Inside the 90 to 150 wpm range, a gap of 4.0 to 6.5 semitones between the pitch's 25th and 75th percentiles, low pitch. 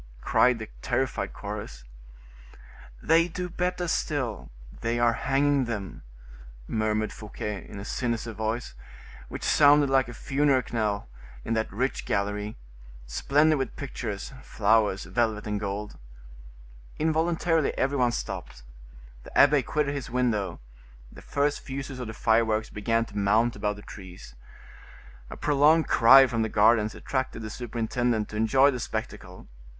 Yes: average, 140 wpm; average, 4.4 semitones; low, 120 Hz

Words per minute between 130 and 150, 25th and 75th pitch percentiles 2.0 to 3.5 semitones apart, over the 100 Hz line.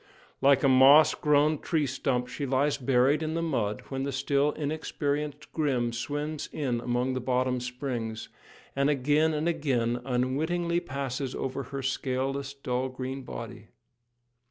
Yes: average, 145 wpm; average, 2.7 semitones; low, 135 Hz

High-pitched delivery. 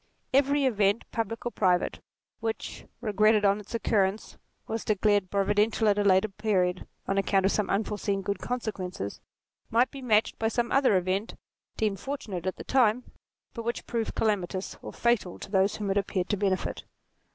Yes: high, 210 Hz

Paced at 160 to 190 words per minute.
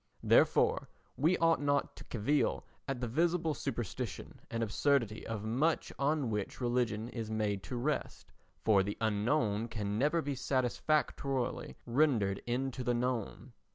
No: average, 140 wpm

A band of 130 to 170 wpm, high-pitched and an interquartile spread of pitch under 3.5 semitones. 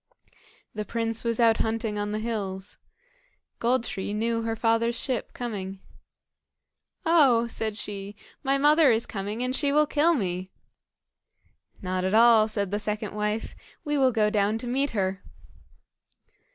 Yes: average, 150 wpm; high, 225 Hz; average, 2.8 semitones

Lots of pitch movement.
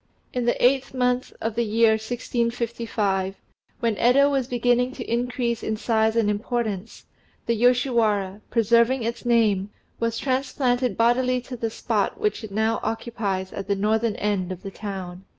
No: average, 2.7 semitones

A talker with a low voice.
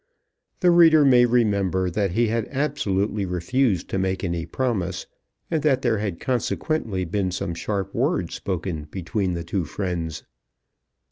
Yes: low, 100 Hz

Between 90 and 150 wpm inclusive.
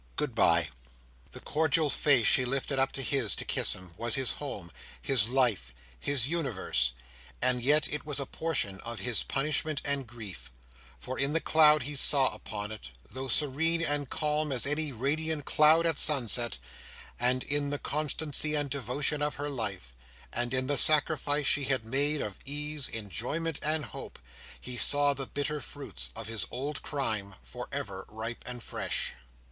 No: average, 165 wpm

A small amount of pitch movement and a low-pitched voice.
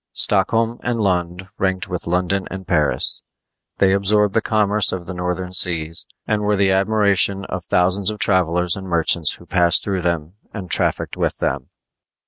Yes: narrow, 2.3 semitones; very low, 95 Hz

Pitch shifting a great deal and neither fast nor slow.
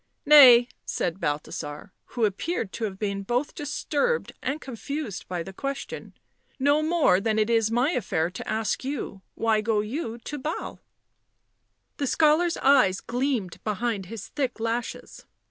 Yes: wide, 5.7 semitones; average, 160 wpm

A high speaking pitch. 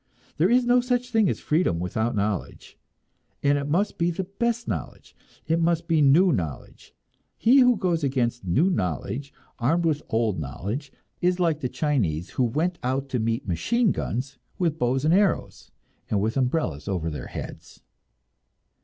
No: medium, 145 Hz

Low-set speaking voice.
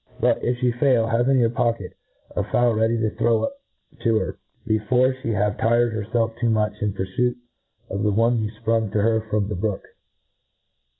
Yes: low, 115 Hz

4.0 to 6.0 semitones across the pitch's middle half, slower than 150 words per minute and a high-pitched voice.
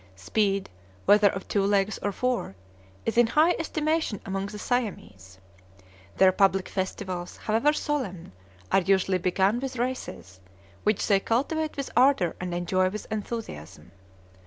Yes: average, 4.6 semitones; slow, 135 wpm; high, 200 Hz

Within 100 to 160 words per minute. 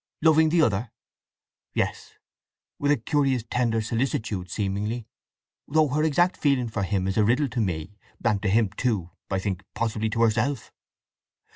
Yes: average, 145 wpm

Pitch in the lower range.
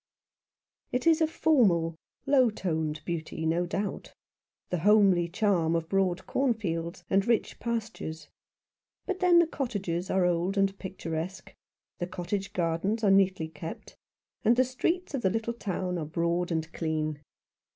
No: high, 190 Hz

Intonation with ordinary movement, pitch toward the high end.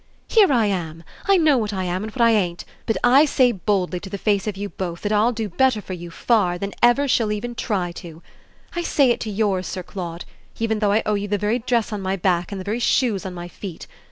Yes: average, 4.0 semitones; high, 205 Hz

